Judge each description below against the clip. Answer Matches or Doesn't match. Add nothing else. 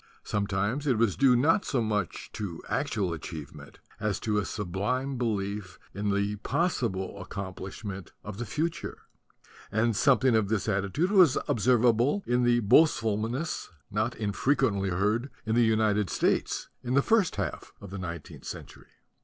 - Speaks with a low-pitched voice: Matches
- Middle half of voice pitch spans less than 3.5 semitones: Doesn't match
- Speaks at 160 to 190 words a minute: Doesn't match